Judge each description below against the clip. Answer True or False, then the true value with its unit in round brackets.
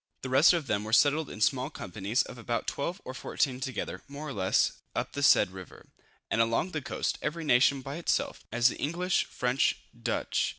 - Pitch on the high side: False (130 Hz)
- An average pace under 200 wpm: False (205 wpm)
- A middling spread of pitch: True (4.6 semitones)